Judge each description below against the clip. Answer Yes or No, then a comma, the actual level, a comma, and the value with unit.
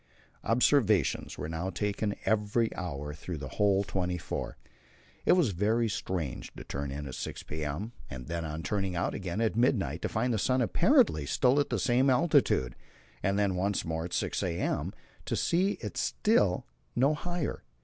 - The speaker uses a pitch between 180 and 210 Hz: No, low, 100 Hz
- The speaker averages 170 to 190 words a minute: Yes, average, 175 wpm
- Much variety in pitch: Yes, wide, 6.5 semitones